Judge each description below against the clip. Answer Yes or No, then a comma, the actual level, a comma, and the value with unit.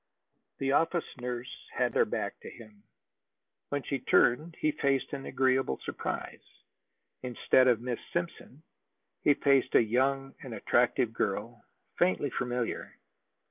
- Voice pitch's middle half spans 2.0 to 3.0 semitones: Yes, narrow, 2.4 semitones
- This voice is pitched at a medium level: No, low, 130 Hz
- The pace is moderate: No, slow, 130 wpm